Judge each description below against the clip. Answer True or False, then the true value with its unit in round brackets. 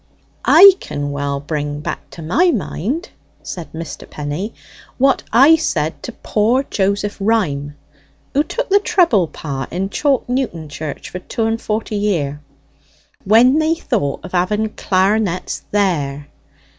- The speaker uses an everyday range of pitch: False (8.2 semitones)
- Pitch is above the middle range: True (200 Hz)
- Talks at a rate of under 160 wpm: True (140 wpm)